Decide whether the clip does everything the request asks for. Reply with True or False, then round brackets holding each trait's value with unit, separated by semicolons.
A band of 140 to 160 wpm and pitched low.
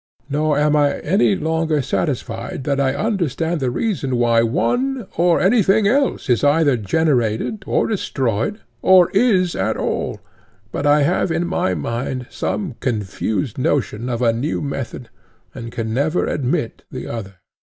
False (150 wpm; 145 Hz)